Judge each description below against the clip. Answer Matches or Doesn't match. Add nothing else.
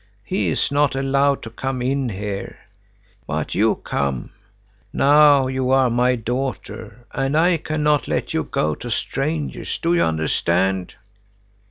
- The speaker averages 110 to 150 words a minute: Matches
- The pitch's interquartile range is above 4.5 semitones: Doesn't match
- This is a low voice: Matches